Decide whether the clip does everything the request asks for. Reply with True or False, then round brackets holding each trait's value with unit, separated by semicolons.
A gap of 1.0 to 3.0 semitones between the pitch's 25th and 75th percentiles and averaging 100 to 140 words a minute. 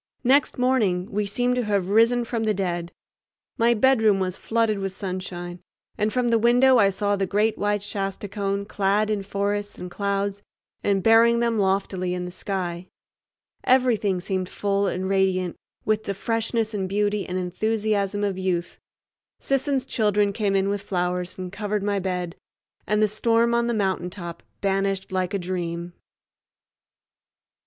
False (2.6 semitones; 160 wpm)